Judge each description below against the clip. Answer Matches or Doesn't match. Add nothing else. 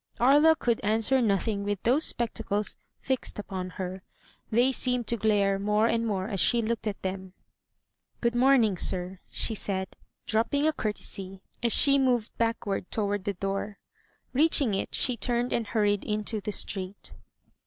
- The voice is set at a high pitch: Matches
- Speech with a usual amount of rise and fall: Matches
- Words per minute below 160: Doesn't match